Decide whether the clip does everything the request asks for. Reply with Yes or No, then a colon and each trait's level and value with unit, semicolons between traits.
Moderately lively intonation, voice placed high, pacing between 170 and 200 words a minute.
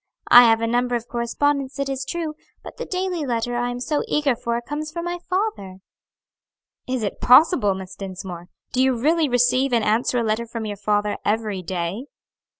Yes: average, 4.6 semitones; high, 245 Hz; average, 190 wpm